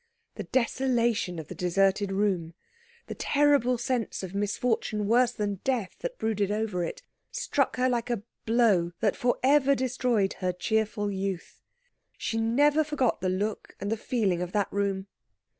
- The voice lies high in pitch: Yes, high, 220 Hz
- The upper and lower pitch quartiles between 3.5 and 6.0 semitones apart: Yes, average, 4.2 semitones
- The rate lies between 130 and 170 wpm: Yes, average, 160 wpm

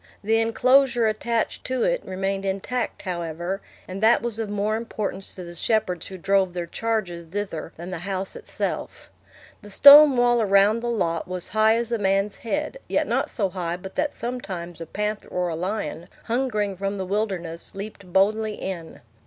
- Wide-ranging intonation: No, average, 3.7 semitones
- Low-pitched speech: No, high, 200 Hz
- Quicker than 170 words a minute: Yes, average, 180 wpm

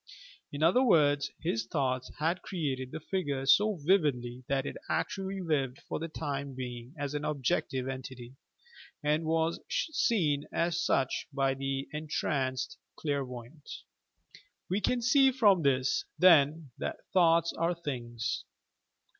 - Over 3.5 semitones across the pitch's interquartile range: Yes, average, 4.2 semitones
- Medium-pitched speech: Yes, medium, 145 Hz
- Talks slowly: Yes, slow, 130 wpm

